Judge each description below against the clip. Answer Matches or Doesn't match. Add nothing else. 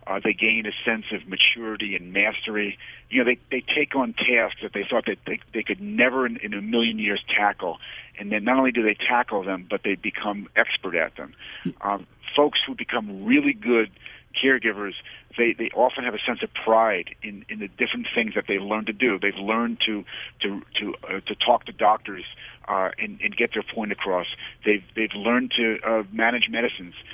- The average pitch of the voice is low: Matches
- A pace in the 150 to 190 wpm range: Doesn't match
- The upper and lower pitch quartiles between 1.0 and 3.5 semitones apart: Matches